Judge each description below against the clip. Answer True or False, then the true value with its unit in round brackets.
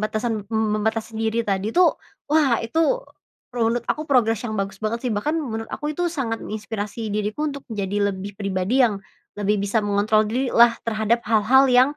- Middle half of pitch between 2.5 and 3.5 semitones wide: True (2.9 semitones)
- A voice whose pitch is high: True (220 Hz)